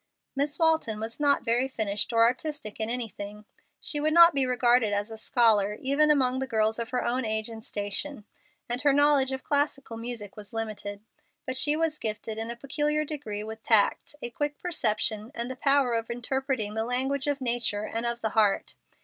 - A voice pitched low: No, high, 240 Hz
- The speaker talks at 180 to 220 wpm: Yes, average, 195 wpm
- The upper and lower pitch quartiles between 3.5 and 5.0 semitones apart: Yes, average, 4.2 semitones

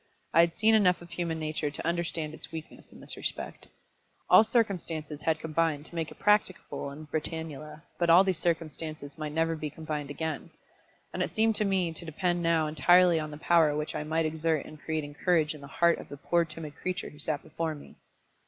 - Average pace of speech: No, fast, 210 wpm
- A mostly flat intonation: Yes, narrow, 2.0 semitones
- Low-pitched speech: No, medium, 160 Hz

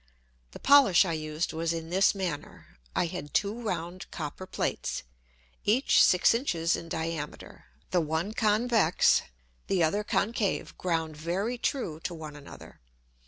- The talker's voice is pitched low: No, medium, 175 Hz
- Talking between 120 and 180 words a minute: Yes, average, 140 wpm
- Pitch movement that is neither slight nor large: Yes, average, 4.3 semitones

